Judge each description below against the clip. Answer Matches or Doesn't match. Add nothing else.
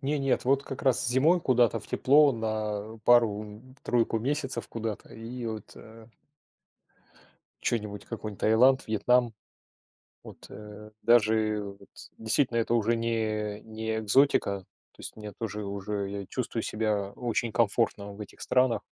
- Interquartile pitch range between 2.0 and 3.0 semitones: Matches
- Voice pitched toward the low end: Matches